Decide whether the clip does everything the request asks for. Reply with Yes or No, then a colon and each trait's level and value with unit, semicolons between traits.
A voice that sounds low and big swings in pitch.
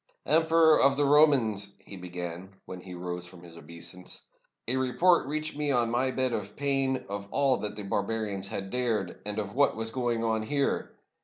Yes: low, 115 Hz; wide, 5.9 semitones